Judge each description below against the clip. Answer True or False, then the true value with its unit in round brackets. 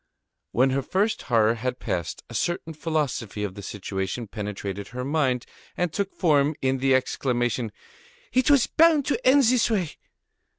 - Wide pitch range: True (7.8 semitones)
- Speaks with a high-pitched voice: False (130 Hz)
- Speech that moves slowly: False (170 wpm)